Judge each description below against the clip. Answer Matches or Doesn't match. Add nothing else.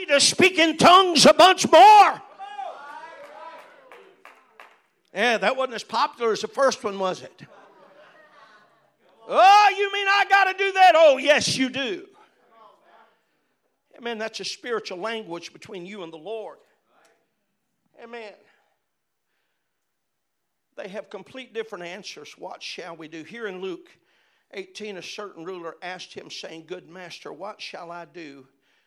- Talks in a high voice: Matches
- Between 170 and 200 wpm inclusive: Doesn't match